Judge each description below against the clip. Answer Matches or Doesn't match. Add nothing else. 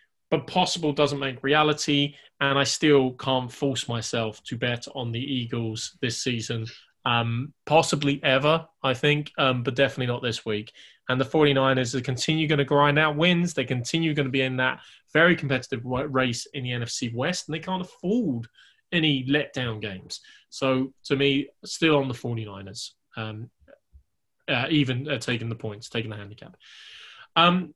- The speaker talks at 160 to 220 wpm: Matches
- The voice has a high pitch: Doesn't match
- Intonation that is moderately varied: Matches